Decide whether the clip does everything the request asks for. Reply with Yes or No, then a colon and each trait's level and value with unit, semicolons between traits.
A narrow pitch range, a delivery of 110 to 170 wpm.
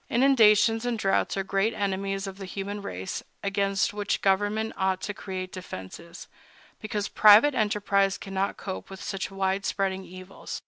Yes: narrow, 1.4 semitones; average, 150 wpm